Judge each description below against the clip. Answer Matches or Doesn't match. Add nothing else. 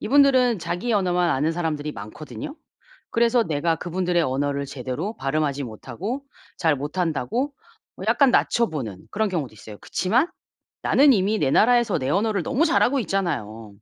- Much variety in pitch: Matches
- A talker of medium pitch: Matches